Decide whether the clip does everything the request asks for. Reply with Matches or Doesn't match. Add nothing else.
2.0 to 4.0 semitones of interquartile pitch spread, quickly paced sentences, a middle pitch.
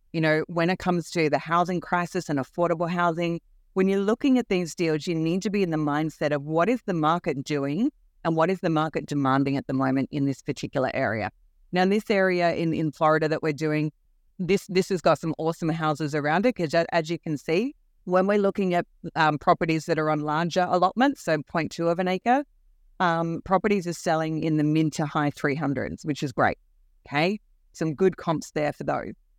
Matches